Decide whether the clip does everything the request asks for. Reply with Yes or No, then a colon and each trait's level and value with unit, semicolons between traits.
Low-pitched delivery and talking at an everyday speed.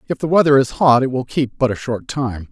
No: low, 130 Hz; fast, 285 wpm